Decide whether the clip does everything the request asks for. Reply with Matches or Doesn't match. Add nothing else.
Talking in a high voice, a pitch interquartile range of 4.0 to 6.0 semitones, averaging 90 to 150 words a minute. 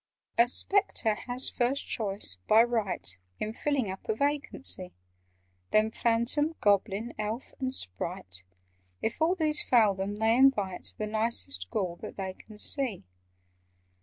Matches